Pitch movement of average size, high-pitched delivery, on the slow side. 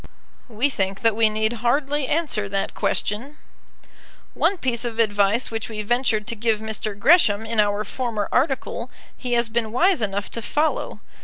No: average, 3.2 semitones; high, 225 Hz; average, 165 wpm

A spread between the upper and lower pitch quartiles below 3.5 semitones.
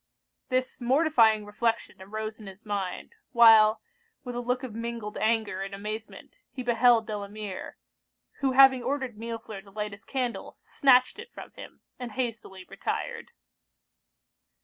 Yes: average, 2.9 semitones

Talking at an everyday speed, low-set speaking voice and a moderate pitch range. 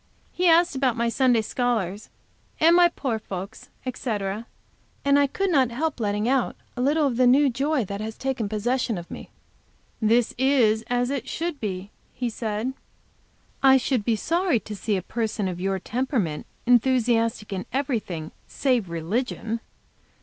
No: average, 160 wpm; high, 240 Hz; average, 4.0 semitones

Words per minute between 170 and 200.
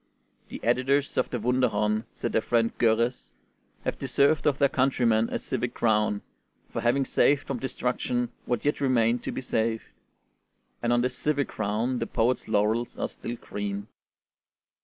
No: average, 160 wpm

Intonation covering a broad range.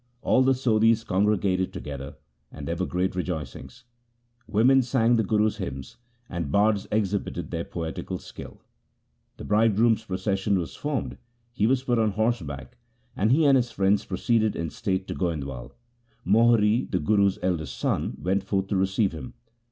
No: average, 3.9 semitones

